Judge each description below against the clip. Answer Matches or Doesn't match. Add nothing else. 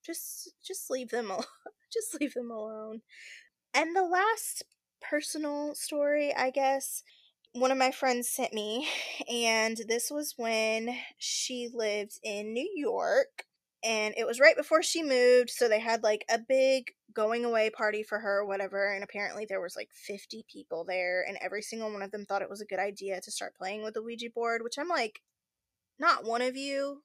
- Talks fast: Doesn't match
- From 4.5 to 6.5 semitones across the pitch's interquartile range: Matches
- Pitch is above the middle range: Matches